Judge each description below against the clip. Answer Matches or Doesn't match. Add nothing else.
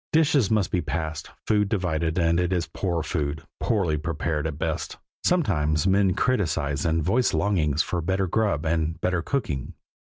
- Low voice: Matches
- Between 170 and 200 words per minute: Doesn't match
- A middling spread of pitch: Matches